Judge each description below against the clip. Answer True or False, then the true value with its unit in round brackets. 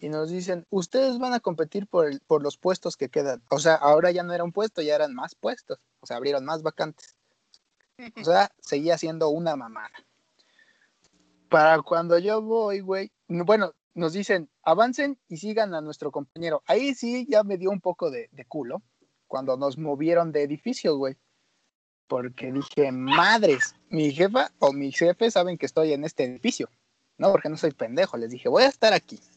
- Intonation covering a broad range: True (6.2 semitones)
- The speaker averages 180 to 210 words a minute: True (190 wpm)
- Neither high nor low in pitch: True (170 Hz)